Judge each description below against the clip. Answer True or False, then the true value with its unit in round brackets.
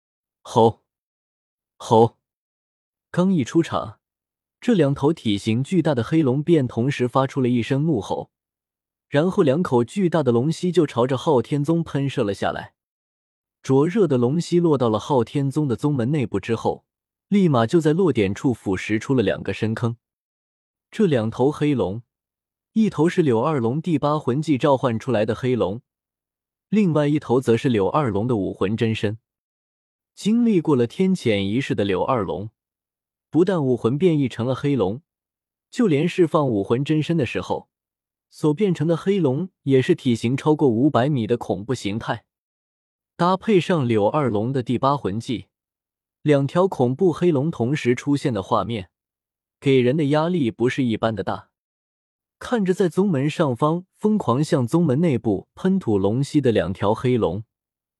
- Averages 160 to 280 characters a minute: True (235 characters per minute)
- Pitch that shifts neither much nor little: False (6.1 semitones)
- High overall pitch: False (135 Hz)